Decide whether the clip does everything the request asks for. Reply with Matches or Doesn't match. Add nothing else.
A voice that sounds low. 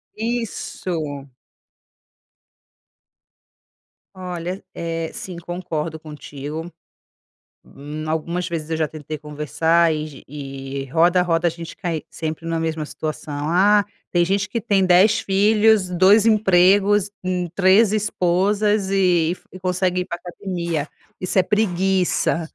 Doesn't match